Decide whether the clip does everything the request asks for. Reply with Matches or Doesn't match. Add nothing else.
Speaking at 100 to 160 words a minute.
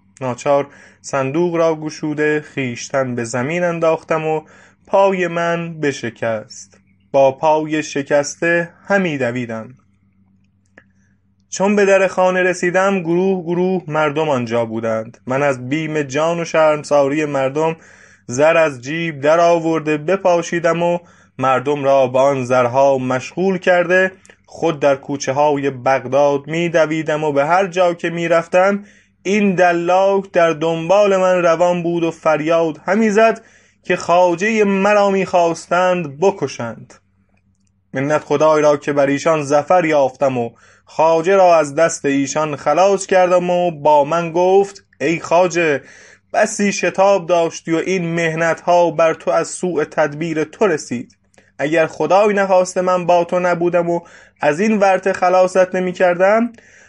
Matches